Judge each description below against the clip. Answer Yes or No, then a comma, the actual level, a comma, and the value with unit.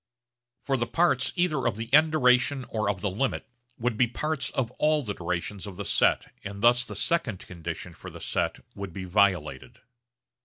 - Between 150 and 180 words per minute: No, average, 190 wpm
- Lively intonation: Yes, wide, 5.8 semitones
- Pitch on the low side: Yes, low, 115 Hz